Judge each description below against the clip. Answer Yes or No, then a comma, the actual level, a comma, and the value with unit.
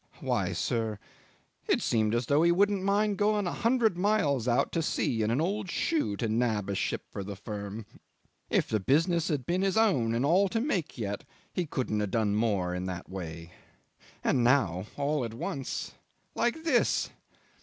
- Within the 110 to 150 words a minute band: No, average, 185 wpm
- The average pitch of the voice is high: No, low, 130 Hz